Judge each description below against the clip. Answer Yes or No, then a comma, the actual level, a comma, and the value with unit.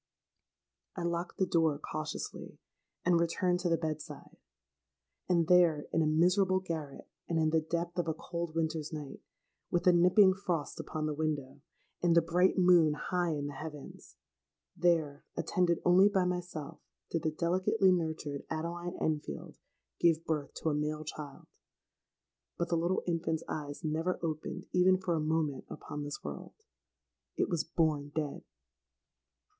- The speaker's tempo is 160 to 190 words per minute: No, average, 150 wpm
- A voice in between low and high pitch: Yes, medium, 165 Hz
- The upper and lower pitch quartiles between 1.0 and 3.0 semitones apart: Yes, narrow, 2.4 semitones